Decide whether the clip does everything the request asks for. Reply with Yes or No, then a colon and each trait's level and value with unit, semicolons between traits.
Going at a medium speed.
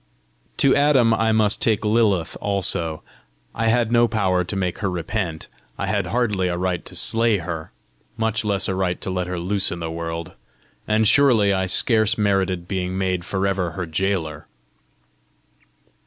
Yes: average, 170 wpm